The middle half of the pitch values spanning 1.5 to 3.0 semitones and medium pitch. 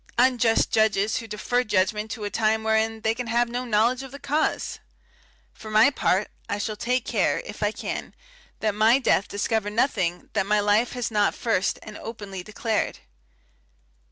No: narrow, 2.4 semitones; high, 220 Hz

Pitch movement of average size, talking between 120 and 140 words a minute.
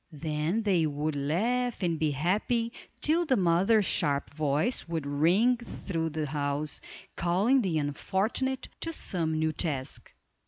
No: wide, 6.5 semitones; slow, 135 wpm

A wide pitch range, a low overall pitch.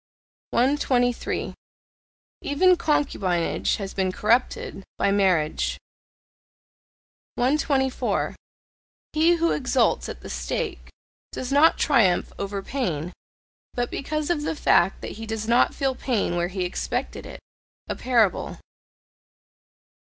No: wide, 6.8 semitones; high, 245 Hz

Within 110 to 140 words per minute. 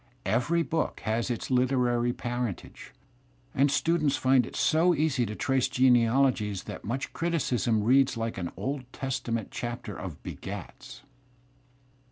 Yes: slow, 135 wpm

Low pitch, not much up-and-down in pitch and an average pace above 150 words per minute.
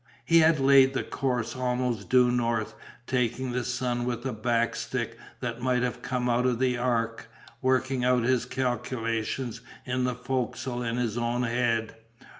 Yes: low, 125 Hz; narrow, 1.4 semitones; average, 165 wpm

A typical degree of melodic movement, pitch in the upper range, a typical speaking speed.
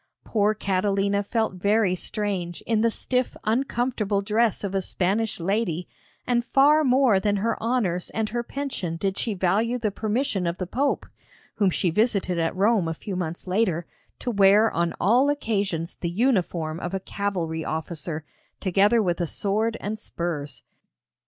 Yes: average, 4.2 semitones; high, 200 Hz; average, 160 wpm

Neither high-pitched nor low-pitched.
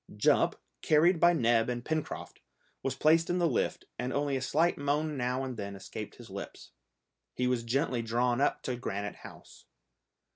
No: low, 130 Hz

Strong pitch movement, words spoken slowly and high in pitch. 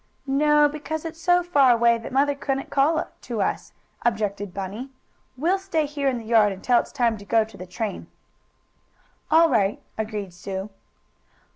No: wide, 5.9 semitones; average, 165 wpm; high, 245 Hz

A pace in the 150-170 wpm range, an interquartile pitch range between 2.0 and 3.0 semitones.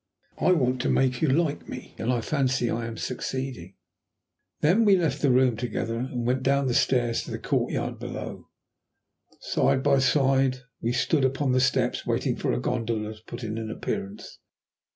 No: average, 180 wpm; narrow, 2.6 semitones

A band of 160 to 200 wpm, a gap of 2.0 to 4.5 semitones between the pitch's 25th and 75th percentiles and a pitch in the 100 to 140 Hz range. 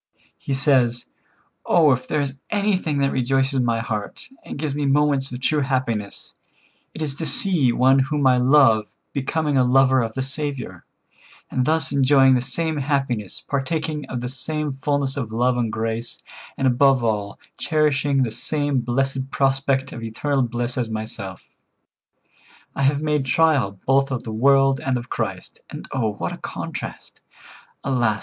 Yes: average, 165 wpm; average, 2.8 semitones; low, 135 Hz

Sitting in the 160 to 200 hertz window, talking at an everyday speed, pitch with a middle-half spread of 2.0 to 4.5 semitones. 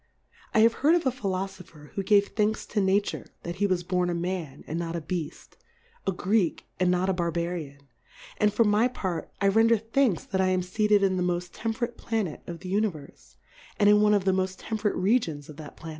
No: high, 190 Hz; fast, 220 wpm; average, 3.4 semitones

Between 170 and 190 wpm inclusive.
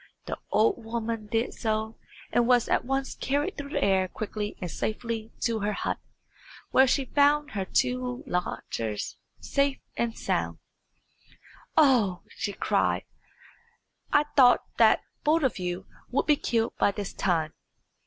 No: average, 145 wpm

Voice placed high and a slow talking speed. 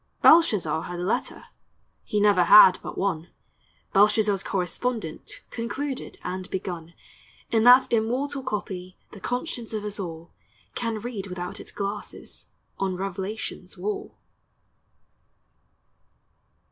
Yes: high, 205 Hz; slow, 110 wpm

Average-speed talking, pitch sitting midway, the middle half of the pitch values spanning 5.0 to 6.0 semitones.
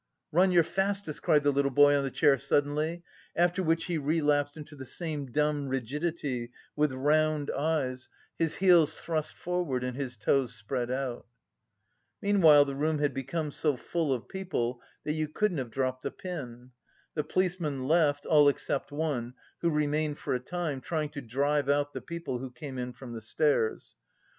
No: average, 175 wpm; medium, 145 Hz; average, 3.3 semitones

